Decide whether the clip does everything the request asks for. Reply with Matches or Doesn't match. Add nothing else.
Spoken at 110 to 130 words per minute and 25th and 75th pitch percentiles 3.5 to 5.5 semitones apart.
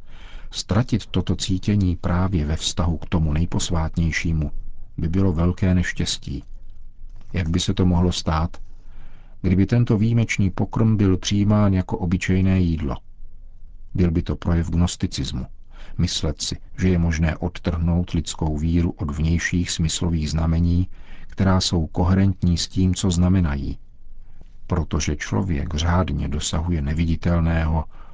Doesn't match